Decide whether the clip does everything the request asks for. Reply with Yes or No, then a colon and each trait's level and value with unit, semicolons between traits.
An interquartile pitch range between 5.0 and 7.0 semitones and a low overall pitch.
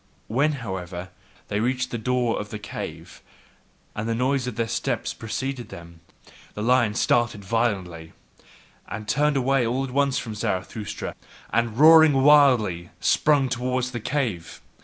No: average, 4.0 semitones; low, 120 Hz